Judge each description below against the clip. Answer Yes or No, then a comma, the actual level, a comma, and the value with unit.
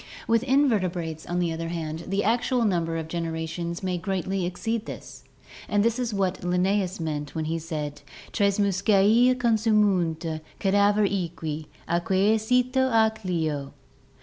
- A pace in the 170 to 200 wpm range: No, average, 145 wpm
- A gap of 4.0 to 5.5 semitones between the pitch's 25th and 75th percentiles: Yes, average, 4.5 semitones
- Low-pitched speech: No, medium, 185 Hz